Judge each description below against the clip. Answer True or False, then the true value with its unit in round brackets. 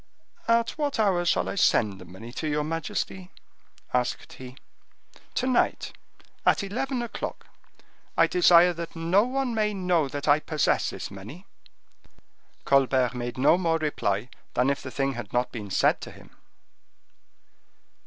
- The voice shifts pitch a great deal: True (7.6 semitones)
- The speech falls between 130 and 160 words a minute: True (150 wpm)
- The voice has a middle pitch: True (155 Hz)